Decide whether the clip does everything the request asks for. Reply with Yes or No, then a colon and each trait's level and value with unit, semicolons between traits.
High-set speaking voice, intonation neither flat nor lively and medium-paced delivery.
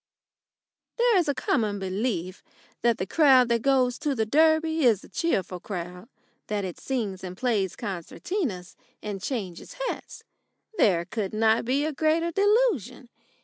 No: high, 235 Hz; wide, 8.1 semitones; average, 145 wpm